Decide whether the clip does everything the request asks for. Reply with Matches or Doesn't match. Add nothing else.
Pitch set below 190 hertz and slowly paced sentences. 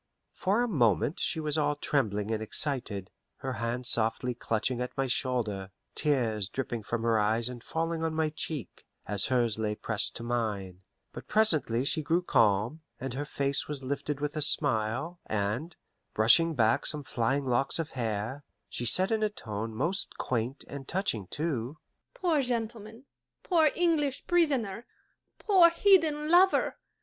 Doesn't match